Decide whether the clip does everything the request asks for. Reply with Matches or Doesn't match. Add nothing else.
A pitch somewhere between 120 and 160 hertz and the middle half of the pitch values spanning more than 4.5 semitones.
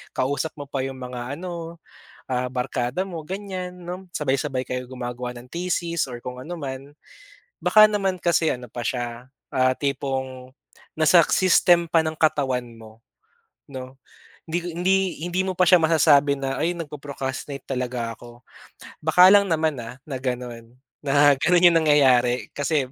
Matches